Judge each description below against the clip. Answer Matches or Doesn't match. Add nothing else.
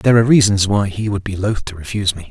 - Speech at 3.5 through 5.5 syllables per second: Doesn't match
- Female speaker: Doesn't match